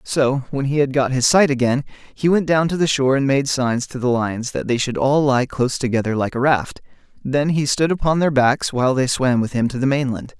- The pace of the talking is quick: Yes, fast, 255 wpm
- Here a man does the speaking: Yes, male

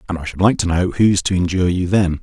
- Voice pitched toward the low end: Yes, very low, 90 Hz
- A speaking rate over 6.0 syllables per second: Yes, 6.5 syllables/s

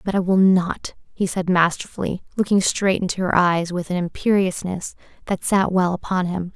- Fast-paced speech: No, average, 185 wpm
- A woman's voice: Yes, female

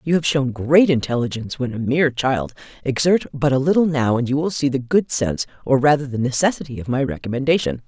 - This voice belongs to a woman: Yes, female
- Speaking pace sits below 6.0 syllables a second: No, 6.1 syllables/s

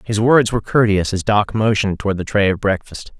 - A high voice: No, low, 105 Hz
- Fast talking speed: Yes, fast, 225 wpm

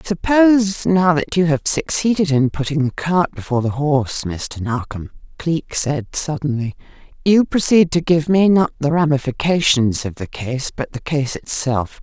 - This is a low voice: No, medium, 150 Hz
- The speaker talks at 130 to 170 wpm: Yes, average, 165 wpm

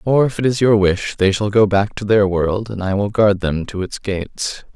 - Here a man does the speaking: Yes, male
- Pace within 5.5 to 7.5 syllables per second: No, 4.8 syllables/s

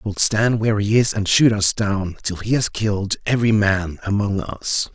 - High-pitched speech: No, low, 105 Hz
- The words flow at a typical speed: No, fast, 220 wpm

